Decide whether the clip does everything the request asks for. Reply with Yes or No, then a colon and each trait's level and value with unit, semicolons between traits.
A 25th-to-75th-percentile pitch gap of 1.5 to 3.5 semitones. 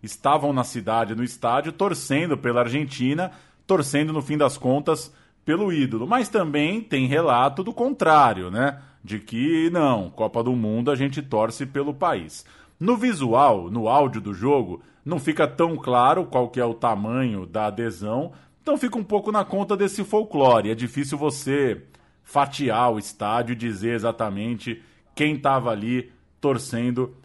No: average, 5.0 semitones